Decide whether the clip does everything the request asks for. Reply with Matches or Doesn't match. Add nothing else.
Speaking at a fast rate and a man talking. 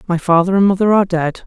Doesn't match